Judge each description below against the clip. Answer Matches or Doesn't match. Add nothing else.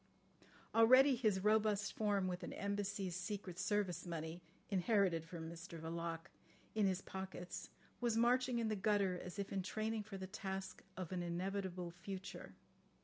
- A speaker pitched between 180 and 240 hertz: Matches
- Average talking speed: Matches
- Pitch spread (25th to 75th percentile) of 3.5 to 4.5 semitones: Doesn't match